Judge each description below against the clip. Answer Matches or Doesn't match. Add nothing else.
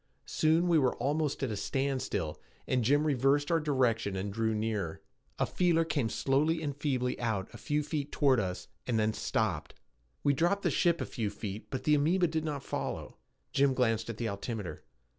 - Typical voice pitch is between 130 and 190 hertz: Matches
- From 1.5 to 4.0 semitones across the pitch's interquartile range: Doesn't match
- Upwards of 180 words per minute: Matches